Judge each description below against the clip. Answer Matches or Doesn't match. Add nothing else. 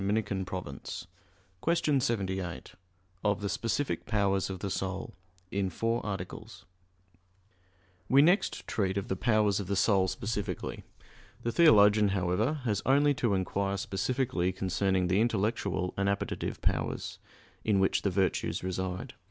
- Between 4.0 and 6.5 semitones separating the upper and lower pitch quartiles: Doesn't match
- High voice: Doesn't match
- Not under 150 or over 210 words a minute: Doesn't match